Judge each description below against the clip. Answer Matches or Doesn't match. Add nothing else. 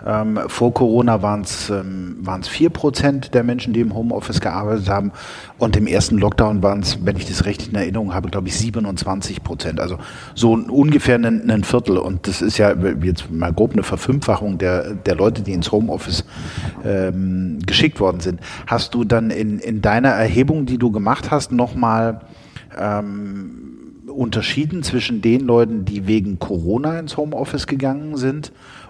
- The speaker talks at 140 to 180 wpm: Matches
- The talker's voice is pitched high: Doesn't match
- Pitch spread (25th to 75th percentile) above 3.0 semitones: Matches